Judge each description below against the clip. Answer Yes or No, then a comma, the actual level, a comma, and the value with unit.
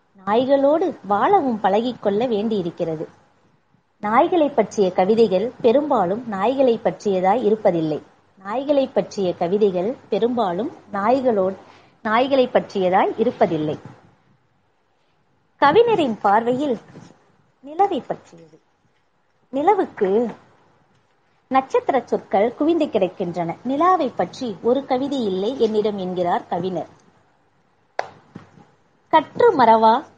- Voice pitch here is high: Yes, high, 225 Hz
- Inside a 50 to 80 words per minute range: Yes, slow, 75 wpm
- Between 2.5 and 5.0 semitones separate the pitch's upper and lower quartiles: No, wide, 5.4 semitones